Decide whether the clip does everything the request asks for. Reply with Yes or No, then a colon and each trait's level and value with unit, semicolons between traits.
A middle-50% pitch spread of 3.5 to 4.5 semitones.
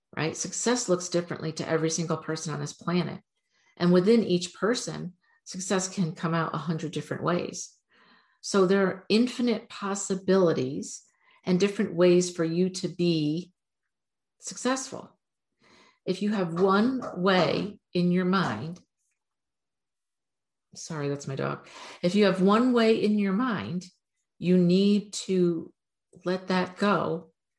No: average, 3.0 semitones